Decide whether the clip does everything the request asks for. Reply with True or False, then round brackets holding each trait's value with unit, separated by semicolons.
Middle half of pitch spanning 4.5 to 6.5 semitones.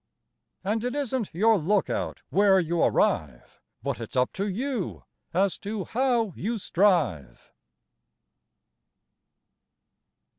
True (5.1 semitones)